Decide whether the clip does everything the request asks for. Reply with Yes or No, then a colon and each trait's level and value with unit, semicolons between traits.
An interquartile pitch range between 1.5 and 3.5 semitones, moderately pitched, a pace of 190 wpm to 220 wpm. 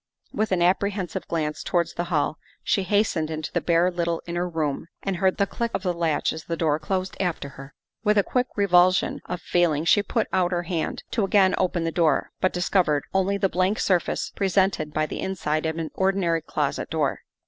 Yes: average, 3.0 semitones; medium, 175 Hz; fast, 205 wpm